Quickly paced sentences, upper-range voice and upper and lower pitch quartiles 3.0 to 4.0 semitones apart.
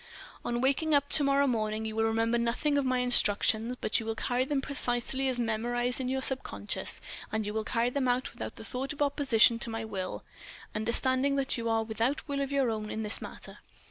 Yes: fast, 210 wpm; high, 240 Hz; average, 3.3 semitones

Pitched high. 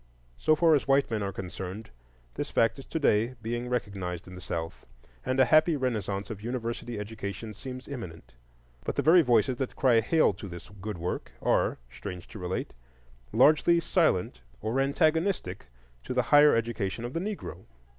No: low, 115 Hz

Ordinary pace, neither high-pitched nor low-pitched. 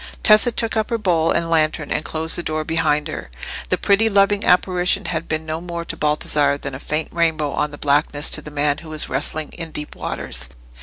No: fast, 215 wpm; medium, 160 Hz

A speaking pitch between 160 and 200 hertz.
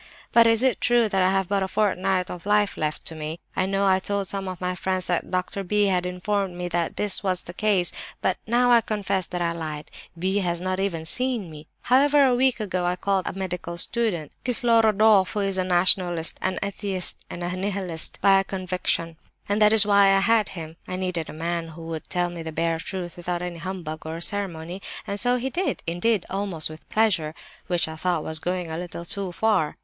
Yes: medium, 185 Hz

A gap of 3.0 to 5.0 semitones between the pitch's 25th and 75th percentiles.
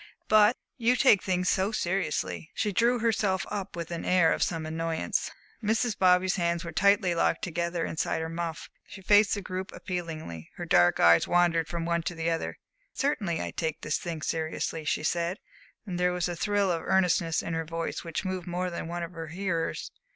No: narrow, 2.5 semitones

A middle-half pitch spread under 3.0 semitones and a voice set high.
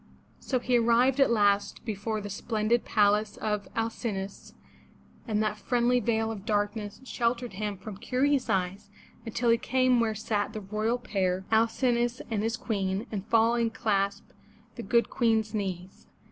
Yes: narrow, 2.5 semitones; high, 220 Hz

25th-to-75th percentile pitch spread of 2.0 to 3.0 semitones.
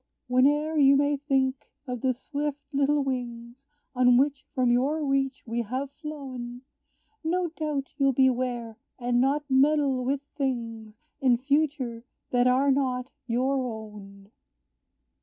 Yes: narrow, 2.5 semitones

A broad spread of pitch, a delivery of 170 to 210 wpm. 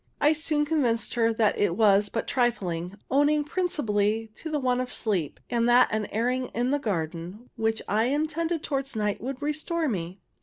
Yes: wide, 5.7 semitones; average, 180 wpm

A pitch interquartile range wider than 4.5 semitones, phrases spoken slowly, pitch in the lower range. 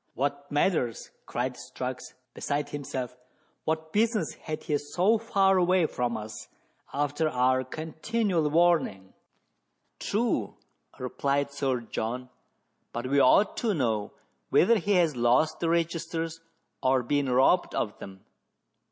No: average, 5.1 semitones; slow, 130 wpm; medium, 145 Hz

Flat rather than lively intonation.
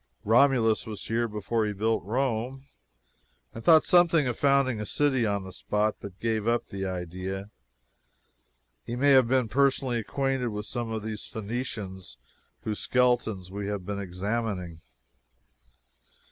No: average, 3.8 semitones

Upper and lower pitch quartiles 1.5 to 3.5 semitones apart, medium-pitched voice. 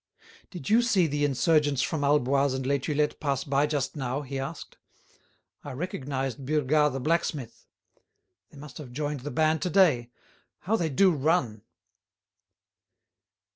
Yes: narrow, 2.6 semitones; medium, 145 Hz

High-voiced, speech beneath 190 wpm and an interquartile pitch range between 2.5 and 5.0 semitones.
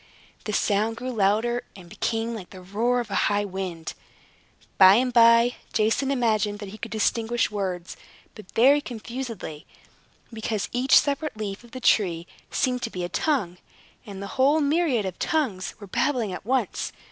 Yes: high, 225 Hz; average, 170 wpm; average, 3.9 semitones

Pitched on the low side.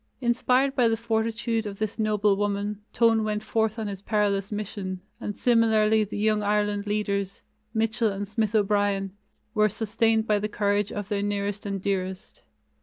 No: high, 210 Hz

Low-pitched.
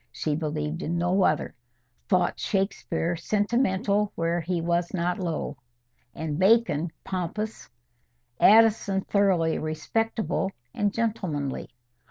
No: medium, 180 Hz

